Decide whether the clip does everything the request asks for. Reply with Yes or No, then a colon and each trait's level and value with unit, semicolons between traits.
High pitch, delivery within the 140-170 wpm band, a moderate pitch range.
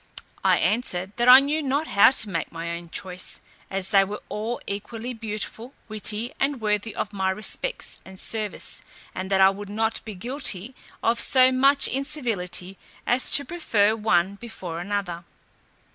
Yes: high, 215 Hz; average, 160 wpm; average, 4.5 semitones